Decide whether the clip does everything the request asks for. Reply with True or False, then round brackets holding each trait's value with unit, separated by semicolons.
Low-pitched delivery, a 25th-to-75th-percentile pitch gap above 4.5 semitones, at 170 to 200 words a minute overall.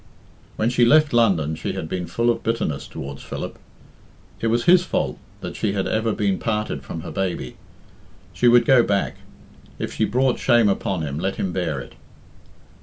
True (105 Hz; 5.6 semitones; 180 wpm)